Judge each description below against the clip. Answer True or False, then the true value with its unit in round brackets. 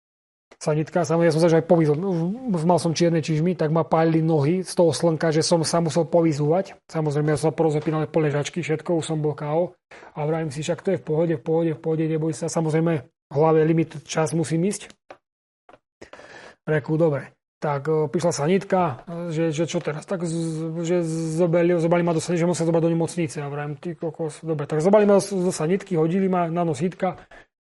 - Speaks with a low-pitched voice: False (165 Hz)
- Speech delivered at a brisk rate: True (195 wpm)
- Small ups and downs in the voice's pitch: True (1.6 semitones)